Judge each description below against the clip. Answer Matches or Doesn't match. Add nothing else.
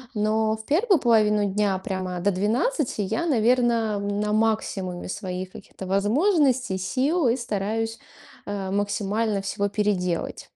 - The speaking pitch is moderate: Doesn't match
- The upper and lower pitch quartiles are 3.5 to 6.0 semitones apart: Doesn't match